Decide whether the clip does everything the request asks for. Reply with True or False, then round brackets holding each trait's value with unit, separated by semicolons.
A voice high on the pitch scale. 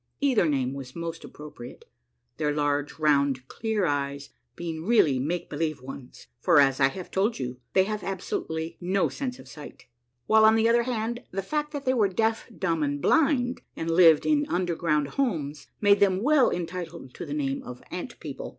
False (170 Hz)